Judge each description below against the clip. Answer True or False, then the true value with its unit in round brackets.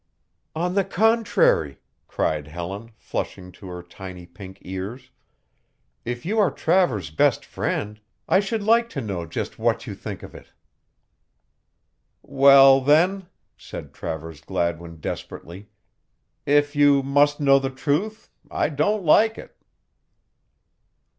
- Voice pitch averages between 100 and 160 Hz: True (135 Hz)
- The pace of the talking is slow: True (125 wpm)